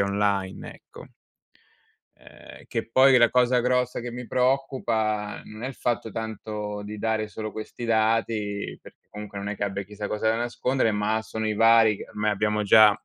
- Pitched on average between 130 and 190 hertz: No, low, 110 Hz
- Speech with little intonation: Yes, narrow, 2.1 semitones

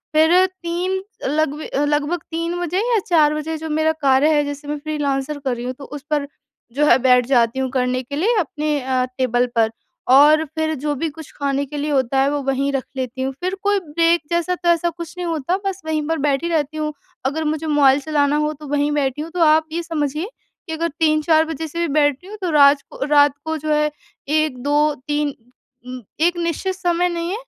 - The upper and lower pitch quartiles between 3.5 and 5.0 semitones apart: No, average, 2.8 semitones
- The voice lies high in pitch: Yes, very high, 300 Hz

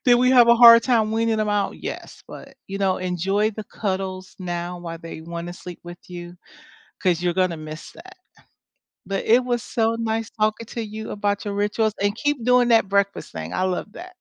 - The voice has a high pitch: Yes, high, 205 Hz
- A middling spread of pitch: Yes, average, 4.1 semitones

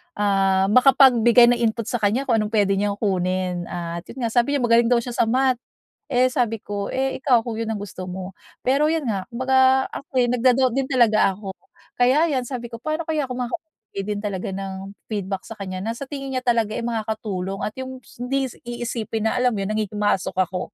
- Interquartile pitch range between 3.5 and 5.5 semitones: Yes, average, 4.3 semitones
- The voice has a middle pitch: No, high, 230 Hz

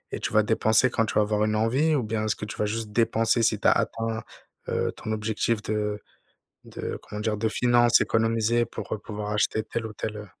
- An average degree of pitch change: No, narrow, 1.2 semitones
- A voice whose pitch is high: No, low, 110 Hz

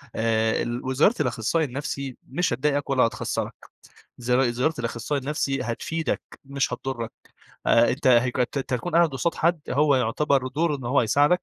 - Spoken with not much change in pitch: No, average, 3.5 semitones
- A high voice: No, low, 135 Hz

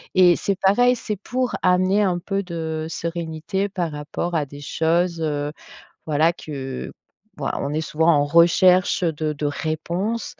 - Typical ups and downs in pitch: Yes, average, 3.2 semitones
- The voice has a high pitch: No, medium, 170 Hz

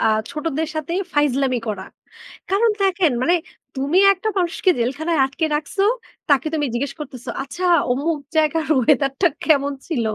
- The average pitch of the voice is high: Yes, very high, 295 Hz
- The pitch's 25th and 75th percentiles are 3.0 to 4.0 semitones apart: Yes, average, 3.5 semitones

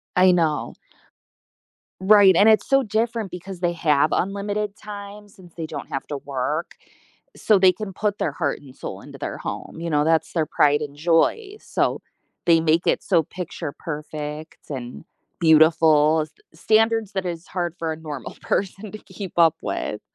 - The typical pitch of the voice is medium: Yes, medium, 170 Hz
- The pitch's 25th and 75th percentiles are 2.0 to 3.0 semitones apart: No, average, 4.5 semitones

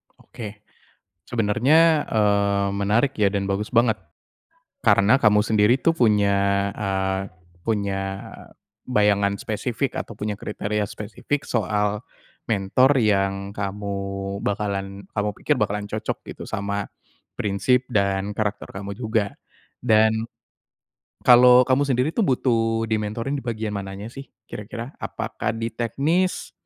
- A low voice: Yes, low, 105 Hz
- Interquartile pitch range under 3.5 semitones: Yes, average, 2.8 semitones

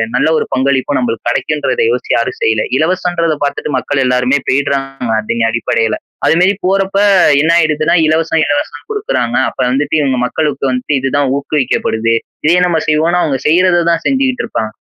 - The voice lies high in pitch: No, medium, 145 Hz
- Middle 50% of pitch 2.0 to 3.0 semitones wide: No, average, 4.4 semitones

